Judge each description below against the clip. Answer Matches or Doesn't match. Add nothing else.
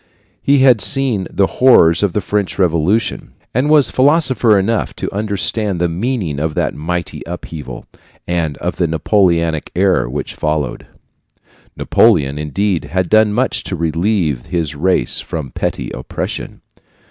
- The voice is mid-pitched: Doesn't match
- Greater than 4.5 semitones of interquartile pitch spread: Matches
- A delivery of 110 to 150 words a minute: Matches